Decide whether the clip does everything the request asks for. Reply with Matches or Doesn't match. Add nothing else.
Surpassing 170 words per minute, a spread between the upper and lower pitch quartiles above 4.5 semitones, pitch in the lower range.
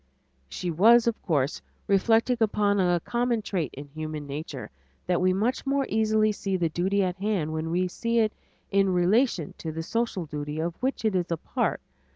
Doesn't match